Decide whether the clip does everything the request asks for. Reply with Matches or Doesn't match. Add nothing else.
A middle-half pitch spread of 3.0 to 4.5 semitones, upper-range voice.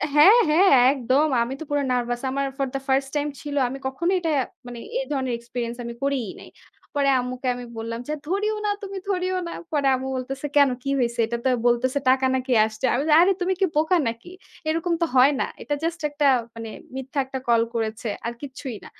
Matches